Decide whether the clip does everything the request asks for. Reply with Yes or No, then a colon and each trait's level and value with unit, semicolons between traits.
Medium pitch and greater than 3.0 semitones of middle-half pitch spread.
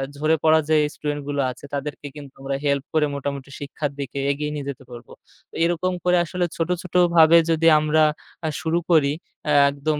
No: medium, 150 Hz; narrow, 2.4 semitones